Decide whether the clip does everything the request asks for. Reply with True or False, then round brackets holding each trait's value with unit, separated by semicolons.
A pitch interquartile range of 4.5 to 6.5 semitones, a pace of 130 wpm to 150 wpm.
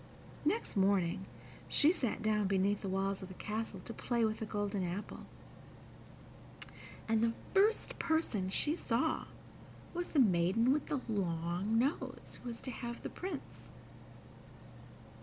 True (5.0 semitones; 140 wpm)